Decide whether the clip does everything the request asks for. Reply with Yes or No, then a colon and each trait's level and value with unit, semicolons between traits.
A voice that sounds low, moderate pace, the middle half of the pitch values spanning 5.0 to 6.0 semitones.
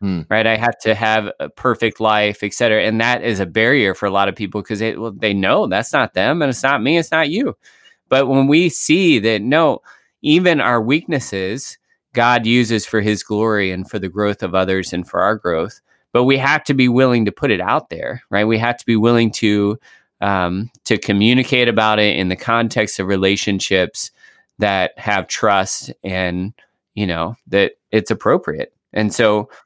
No: low, 110 Hz; average, 195 wpm; average, 3.3 semitones